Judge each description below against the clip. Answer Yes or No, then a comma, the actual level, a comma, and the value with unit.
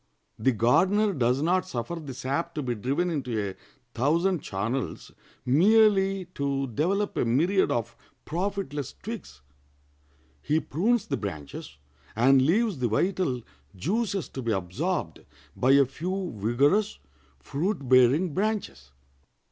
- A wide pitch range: Yes, wide, 7.5 semitones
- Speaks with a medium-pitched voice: Yes, medium, 145 Hz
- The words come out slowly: Yes, slow, 125 wpm